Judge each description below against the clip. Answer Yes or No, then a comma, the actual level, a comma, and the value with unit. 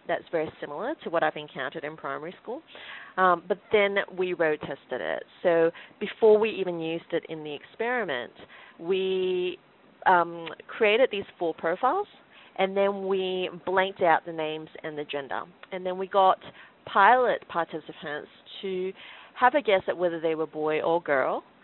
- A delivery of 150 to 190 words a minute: Yes, average, 165 wpm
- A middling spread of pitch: Yes, average, 3.6 semitones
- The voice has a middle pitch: Yes, medium, 180 Hz